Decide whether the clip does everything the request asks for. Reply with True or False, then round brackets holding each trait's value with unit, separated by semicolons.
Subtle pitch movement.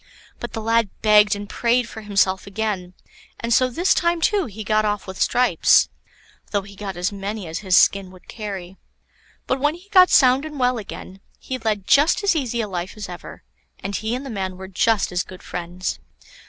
False (4.6 semitones)